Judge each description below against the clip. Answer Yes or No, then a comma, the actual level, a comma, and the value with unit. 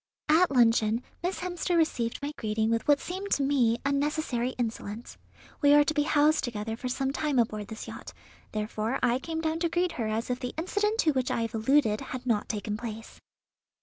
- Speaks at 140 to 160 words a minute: No, average, 200 wpm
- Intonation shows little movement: No, average, 5.3 semitones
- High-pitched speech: Yes, very high, 255 Hz